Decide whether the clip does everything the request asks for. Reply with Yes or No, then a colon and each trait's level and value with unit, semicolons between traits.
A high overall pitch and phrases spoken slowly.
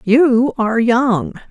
Yes: high, 240 Hz; slow, 120 wpm